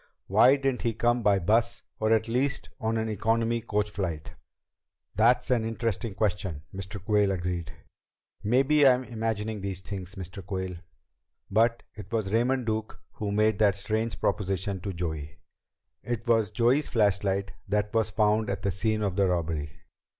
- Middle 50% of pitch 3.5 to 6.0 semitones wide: No, average, 2.8 semitones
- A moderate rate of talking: Yes, average, 155 wpm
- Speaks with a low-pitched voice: Yes, low, 105 Hz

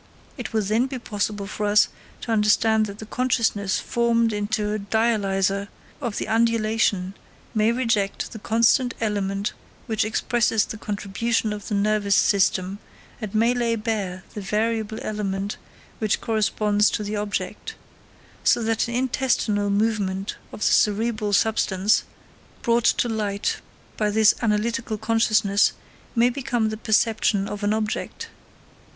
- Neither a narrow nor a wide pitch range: No, narrow, 1.9 semitones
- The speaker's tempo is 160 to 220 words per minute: No, average, 140 wpm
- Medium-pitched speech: No, high, 215 Hz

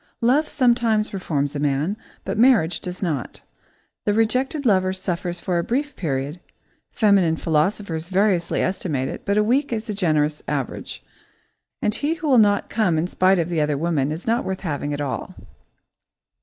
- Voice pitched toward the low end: No, medium, 185 Hz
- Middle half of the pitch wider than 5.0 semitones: Yes, wide, 5.6 semitones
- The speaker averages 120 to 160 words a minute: No, average, 170 wpm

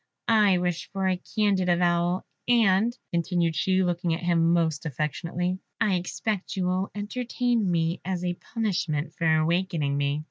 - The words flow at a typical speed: Yes, average, 150 wpm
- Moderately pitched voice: Yes, medium, 180 Hz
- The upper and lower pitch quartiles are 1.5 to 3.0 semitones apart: Yes, narrow, 2.4 semitones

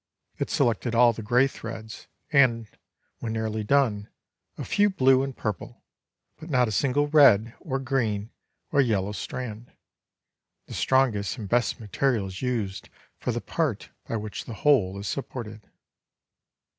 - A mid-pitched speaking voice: No, low, 115 Hz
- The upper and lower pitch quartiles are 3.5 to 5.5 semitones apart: Yes, average, 3.9 semitones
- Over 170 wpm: No, average, 145 wpm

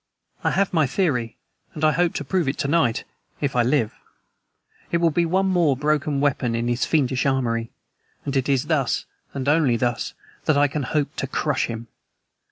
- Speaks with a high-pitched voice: No, medium, 140 Hz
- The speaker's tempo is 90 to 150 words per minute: No, average, 190 wpm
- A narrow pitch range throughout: No, average, 3.9 semitones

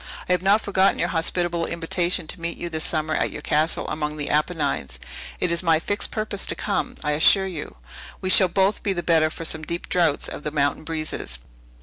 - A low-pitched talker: No, medium, 165 Hz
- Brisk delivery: Yes, fast, 215 wpm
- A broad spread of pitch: No, average, 2.8 semitones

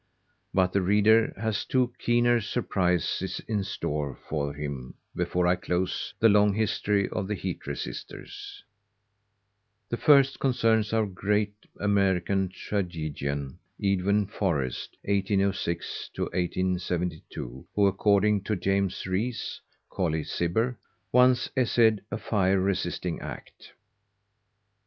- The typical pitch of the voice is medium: No, low, 100 Hz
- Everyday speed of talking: No, slow, 110 wpm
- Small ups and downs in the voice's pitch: No, average, 3.1 semitones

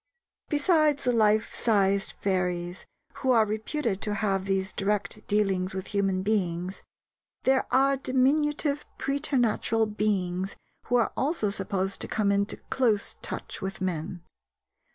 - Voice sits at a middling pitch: No, high, 210 Hz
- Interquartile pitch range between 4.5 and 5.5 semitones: Yes, average, 4.8 semitones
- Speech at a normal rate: No, slow, 130 wpm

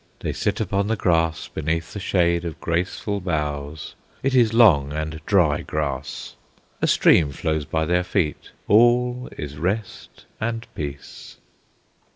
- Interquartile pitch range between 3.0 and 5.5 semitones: Yes, average, 5.1 semitones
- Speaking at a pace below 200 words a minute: Yes, average, 140 wpm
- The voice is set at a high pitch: No, very low, 85 Hz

